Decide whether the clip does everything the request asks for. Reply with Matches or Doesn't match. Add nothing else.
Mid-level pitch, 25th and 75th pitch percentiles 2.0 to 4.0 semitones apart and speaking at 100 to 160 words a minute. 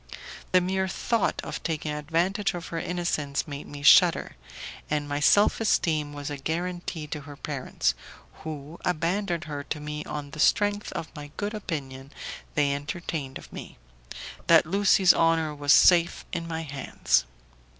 Matches